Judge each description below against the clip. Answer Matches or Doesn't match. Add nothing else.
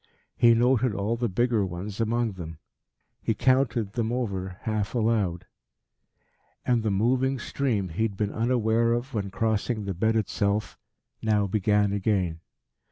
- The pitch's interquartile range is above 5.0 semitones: Doesn't match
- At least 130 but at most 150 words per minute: Matches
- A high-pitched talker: Doesn't match